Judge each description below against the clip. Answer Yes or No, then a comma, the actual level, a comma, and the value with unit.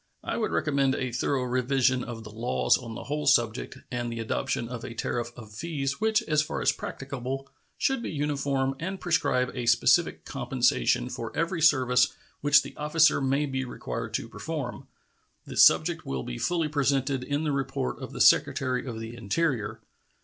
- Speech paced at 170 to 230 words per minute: Yes, average, 180 wpm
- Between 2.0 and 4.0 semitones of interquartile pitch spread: Yes, average, 3.5 semitones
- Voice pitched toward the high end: No, low, 135 Hz